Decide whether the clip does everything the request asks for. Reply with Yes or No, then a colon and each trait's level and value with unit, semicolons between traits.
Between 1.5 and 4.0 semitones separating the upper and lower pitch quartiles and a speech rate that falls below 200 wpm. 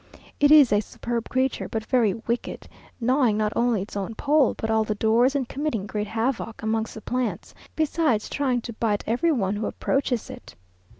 Yes: average, 3.2 semitones; average, 185 wpm